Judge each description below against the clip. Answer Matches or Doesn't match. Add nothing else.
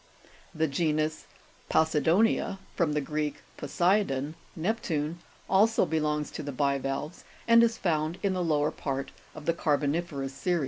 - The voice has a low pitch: Doesn't match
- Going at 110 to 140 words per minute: Matches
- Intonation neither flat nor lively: Matches